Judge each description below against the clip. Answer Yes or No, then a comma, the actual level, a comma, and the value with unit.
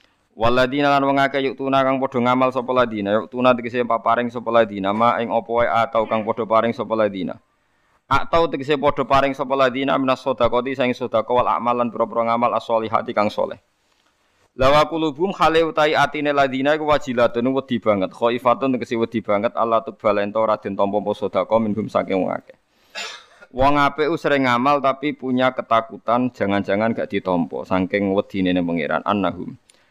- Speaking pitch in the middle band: No, low, 120 Hz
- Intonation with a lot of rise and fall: No, average, 3.4 semitones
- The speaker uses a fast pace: Yes, fast, 165 wpm